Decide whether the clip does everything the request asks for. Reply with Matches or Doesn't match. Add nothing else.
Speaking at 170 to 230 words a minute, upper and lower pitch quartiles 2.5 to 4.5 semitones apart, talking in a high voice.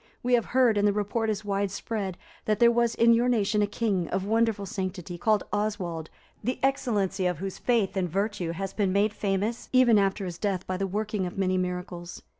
Matches